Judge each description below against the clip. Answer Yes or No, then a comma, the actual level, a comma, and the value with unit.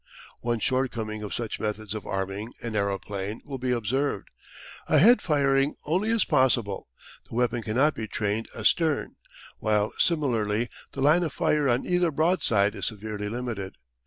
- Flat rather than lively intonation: No, average, 4.9 semitones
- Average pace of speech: Yes, average, 150 wpm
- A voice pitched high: No, low, 120 Hz